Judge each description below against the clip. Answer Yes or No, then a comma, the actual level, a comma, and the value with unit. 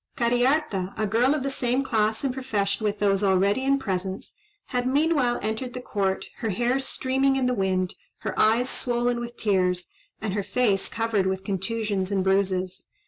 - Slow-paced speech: No, average, 175 wpm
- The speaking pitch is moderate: No, high, 220 Hz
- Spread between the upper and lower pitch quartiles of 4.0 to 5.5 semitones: Yes, average, 4.4 semitones